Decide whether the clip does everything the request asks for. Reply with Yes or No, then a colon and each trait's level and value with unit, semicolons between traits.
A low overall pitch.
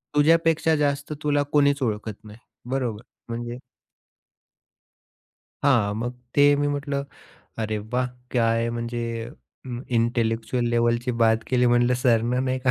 Yes: low, 120 Hz